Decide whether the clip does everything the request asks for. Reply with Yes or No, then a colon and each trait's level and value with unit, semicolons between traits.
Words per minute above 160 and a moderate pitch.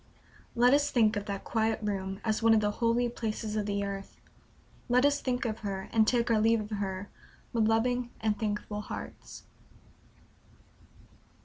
No: average, 170 wpm; high, 220 Hz